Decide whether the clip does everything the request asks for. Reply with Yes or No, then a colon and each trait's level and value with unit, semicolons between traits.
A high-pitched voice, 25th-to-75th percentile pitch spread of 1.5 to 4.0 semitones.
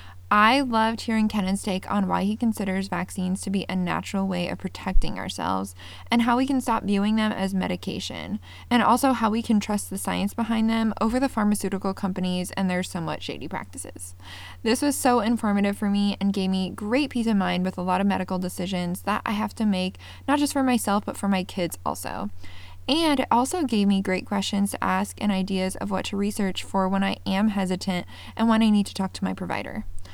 Yes: high, 195 Hz; average, 3.2 semitones